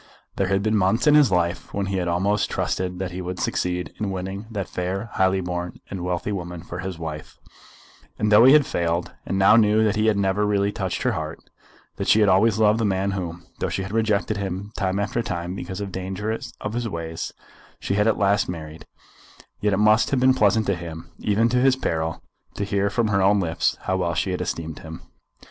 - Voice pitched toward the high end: No, very low, 95 Hz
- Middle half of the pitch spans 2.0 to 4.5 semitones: Yes, average, 2.9 semitones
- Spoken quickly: Yes, fast, 225 wpm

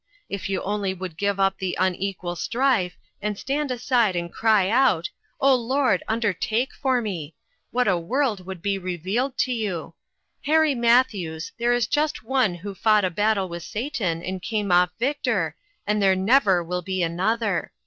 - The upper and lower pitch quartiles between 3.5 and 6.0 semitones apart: Yes, average, 4.9 semitones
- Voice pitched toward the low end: No, high, 205 Hz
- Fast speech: No, average, 175 wpm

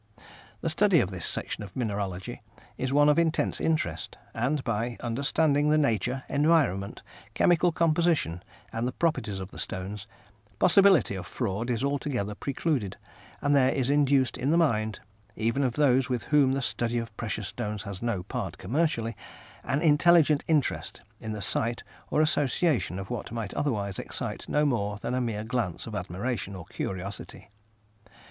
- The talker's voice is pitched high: No, low, 125 Hz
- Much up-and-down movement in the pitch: Yes, wide, 6.0 semitones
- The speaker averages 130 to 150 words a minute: No, average, 160 wpm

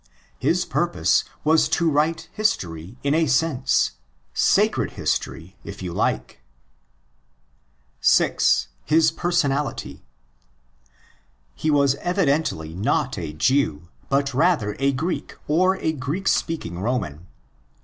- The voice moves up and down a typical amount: No, wide, 9.0 semitones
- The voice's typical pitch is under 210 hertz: Yes, medium, 140 Hz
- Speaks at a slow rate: Yes, slow, 105 wpm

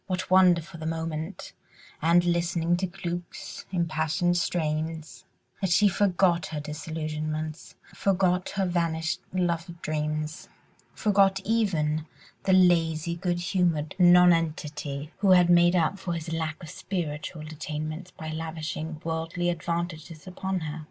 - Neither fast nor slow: No, slow, 125 wpm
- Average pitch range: No, narrow, 2.3 semitones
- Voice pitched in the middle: Yes, medium, 170 Hz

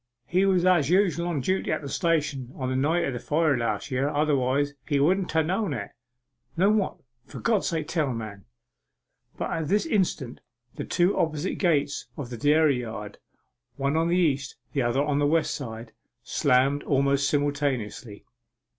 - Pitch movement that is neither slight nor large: Yes, average, 4.3 semitones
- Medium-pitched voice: Yes, medium, 145 Hz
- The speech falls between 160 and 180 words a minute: Yes, average, 175 wpm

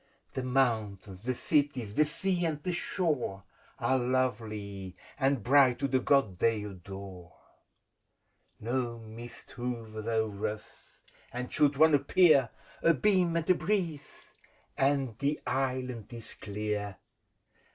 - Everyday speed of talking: No, slow, 125 wpm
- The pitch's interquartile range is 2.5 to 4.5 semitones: No, average, 5.0 semitones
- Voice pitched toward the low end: Yes, low, 125 Hz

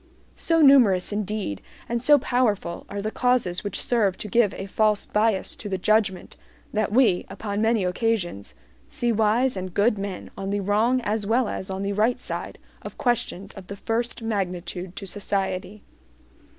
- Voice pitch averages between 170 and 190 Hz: No, high, 210 Hz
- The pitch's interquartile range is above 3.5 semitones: No, average, 3.1 semitones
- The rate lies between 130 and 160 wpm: No, average, 170 wpm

